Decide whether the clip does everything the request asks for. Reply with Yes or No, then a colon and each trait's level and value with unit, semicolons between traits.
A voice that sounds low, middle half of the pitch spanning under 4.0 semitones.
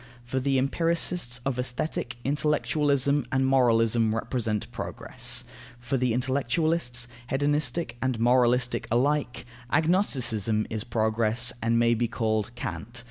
Yes: low, 125 Hz; average, 3.1 semitones